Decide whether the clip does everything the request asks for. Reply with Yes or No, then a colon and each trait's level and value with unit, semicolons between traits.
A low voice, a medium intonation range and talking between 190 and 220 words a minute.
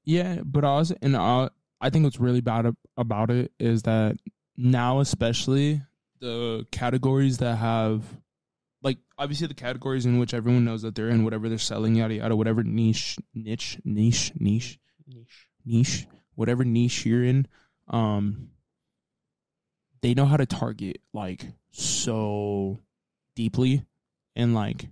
No: low, 120 Hz; average, 3.0 semitones; average, 140 wpm